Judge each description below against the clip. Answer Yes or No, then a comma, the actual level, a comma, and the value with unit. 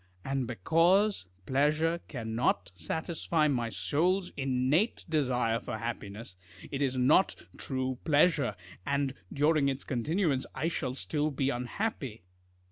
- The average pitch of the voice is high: No, low, 135 Hz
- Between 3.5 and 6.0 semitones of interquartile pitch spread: Yes, average, 4.7 semitones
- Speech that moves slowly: Yes, slow, 120 wpm